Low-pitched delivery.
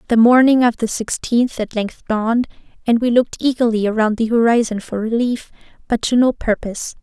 No: high, 230 Hz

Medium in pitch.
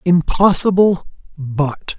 Yes: medium, 170 Hz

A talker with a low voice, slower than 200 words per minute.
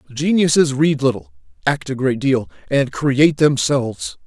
Yes: low, 130 Hz; average, 140 wpm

